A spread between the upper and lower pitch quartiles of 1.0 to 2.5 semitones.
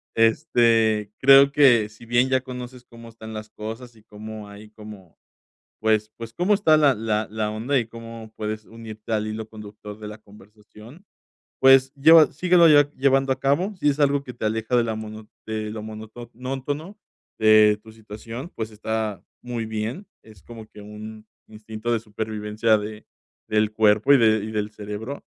No: average, 2.9 semitones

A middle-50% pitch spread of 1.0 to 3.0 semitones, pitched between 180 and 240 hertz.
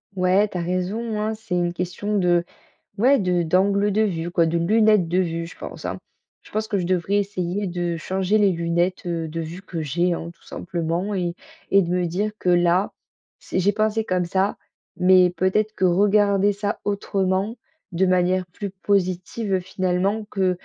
Yes: narrow, 2.6 semitones; medium, 185 Hz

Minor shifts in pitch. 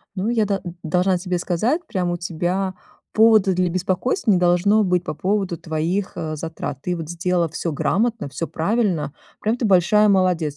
No: average, 3.1 semitones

